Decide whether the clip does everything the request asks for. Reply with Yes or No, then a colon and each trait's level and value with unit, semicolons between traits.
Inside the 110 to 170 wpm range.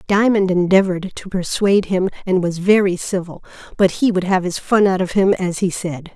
No: fast, 205 wpm